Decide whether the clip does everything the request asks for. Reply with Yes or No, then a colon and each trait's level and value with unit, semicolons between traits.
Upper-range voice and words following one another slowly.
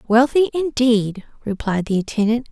Yes: high, 235 Hz; slow, 120 wpm